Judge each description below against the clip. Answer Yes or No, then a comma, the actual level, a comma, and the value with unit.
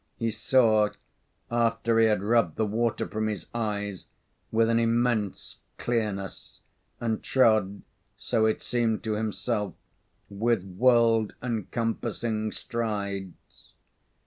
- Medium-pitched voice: No, low, 110 Hz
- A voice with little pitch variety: Yes, narrow, 2.0 semitones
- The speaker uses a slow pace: Yes, slow, 110 wpm